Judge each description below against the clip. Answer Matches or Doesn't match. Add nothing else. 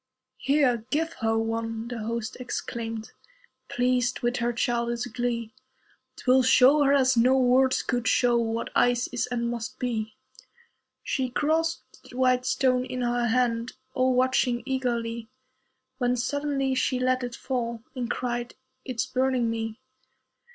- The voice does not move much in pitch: Matches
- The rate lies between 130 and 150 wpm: Matches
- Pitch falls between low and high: Doesn't match